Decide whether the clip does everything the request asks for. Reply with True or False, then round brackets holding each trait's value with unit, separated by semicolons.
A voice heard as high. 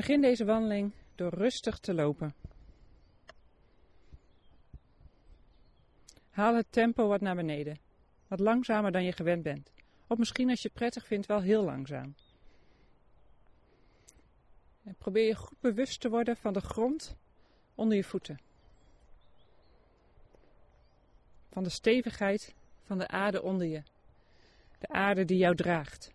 True (200 Hz)